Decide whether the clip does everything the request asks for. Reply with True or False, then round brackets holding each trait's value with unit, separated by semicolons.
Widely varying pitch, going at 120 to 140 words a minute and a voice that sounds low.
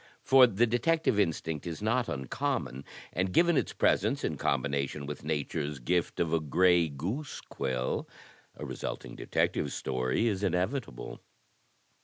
True (7.6 semitones; 135 wpm; 85 Hz)